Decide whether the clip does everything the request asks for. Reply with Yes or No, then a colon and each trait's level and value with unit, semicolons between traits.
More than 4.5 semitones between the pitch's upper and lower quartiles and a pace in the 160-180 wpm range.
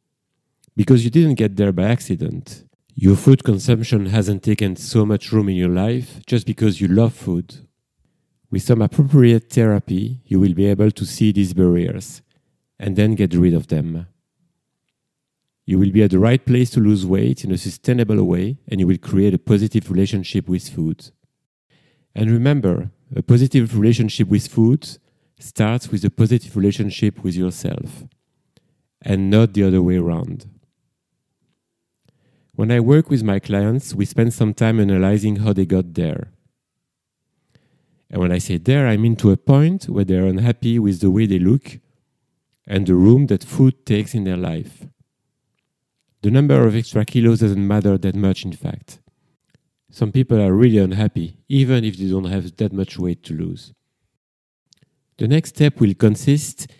Yes: average, 4.9 semitones; average, 165 wpm